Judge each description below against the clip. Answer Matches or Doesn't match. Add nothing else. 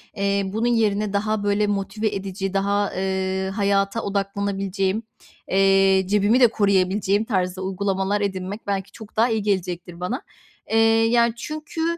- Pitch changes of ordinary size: Doesn't match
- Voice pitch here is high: Matches